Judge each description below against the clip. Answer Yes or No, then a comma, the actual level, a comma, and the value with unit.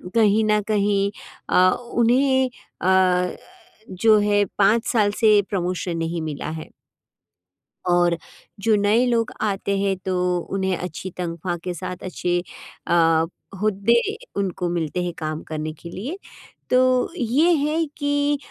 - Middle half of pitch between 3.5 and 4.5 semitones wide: Yes, average, 4.1 semitones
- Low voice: No, high, 195 Hz